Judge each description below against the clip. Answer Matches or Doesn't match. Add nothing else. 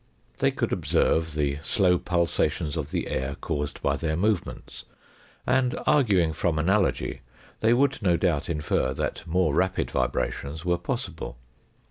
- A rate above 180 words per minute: Doesn't match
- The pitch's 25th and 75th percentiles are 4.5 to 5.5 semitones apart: Doesn't match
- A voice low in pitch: Matches